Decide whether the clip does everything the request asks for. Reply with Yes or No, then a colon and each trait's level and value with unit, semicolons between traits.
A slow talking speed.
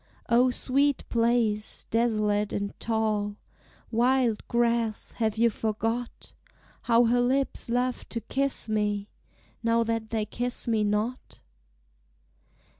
Yes: slow, 115 wpm